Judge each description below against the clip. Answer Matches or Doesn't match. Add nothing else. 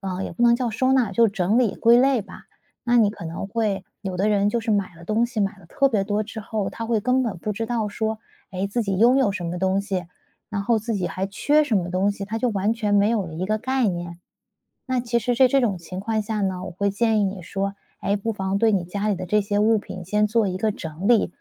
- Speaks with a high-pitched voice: Matches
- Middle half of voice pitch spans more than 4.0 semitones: Doesn't match